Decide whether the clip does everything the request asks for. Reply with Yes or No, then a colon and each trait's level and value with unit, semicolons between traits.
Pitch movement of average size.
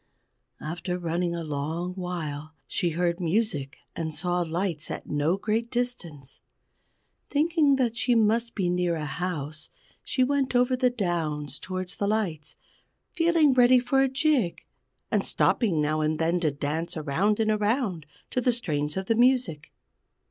No: wide, 7.2 semitones